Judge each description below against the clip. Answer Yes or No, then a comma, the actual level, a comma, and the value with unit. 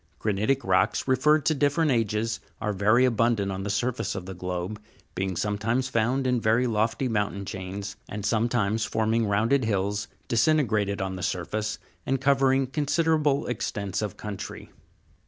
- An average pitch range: Yes, average, 4.3 semitones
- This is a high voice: No, low, 110 Hz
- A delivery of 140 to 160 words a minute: Yes, average, 155 wpm